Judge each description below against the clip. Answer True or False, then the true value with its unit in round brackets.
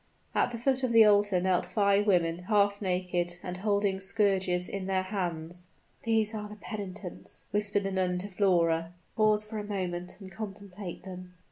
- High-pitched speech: True (195 Hz)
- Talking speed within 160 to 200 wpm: True (170 wpm)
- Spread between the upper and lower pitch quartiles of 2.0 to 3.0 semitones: True (2.5 semitones)